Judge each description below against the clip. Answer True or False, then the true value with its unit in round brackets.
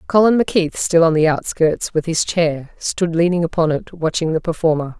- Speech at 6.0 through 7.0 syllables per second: False (5.2 syllables/s)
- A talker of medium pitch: True (165 Hz)